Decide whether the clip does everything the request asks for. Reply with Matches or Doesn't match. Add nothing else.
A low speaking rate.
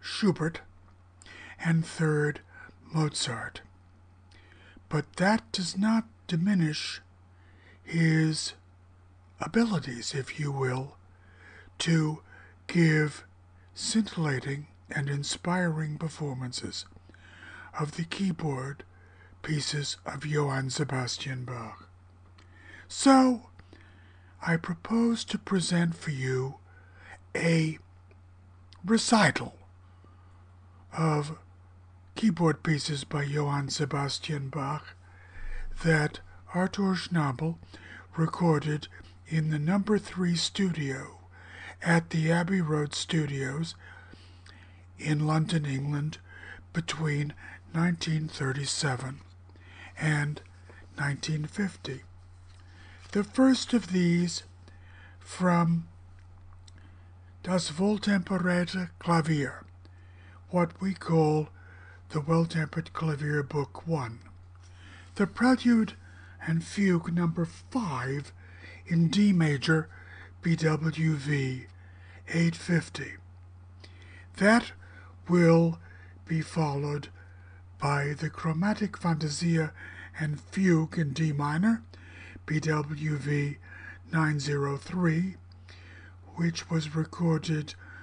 Matches